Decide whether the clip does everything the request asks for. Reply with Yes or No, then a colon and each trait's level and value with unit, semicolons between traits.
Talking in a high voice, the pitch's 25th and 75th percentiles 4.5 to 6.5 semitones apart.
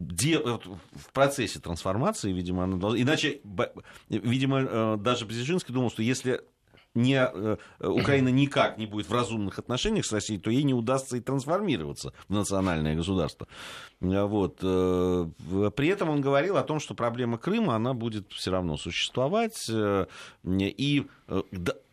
No: low, 110 Hz; wide, 5.5 semitones